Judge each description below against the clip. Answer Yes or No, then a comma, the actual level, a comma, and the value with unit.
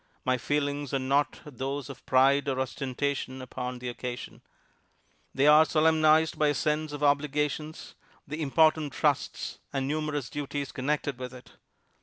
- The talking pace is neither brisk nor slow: Yes, average, 150 wpm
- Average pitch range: No, narrow, 2.3 semitones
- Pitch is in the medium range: Yes, medium, 145 Hz